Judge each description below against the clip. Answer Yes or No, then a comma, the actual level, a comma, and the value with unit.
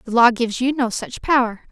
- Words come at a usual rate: No, fast, 245 wpm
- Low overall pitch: No, high, 240 Hz